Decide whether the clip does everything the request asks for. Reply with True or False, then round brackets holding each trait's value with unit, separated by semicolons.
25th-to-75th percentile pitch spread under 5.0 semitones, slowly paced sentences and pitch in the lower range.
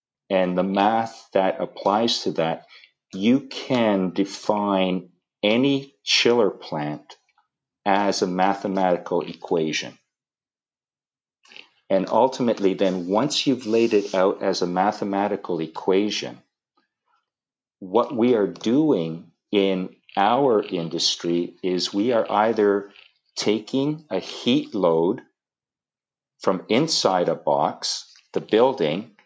True (2.6 semitones; 105 wpm; 100 Hz)